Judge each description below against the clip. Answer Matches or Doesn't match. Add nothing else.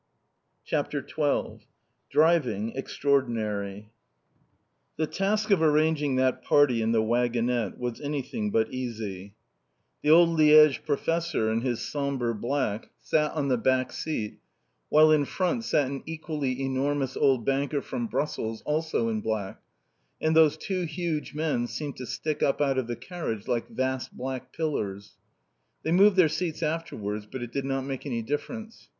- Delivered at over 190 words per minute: Doesn't match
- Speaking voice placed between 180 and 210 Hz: Doesn't match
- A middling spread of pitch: Matches